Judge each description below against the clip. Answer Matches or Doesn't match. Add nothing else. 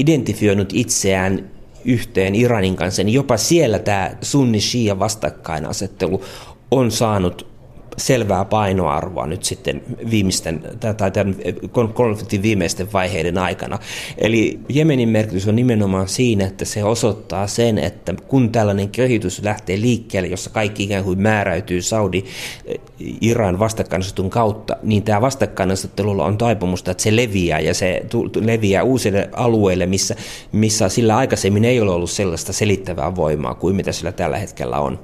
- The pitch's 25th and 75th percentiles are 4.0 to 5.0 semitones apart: Doesn't match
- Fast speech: Doesn't match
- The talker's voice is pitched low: Matches